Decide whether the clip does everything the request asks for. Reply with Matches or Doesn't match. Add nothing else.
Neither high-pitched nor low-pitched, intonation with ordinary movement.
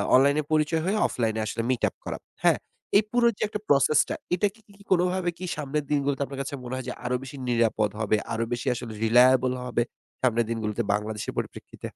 Doesn't match